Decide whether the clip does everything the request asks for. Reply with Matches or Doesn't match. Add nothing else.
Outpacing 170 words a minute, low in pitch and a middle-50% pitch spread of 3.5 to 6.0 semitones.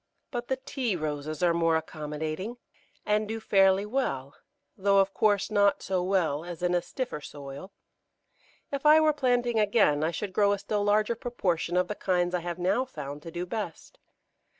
Doesn't match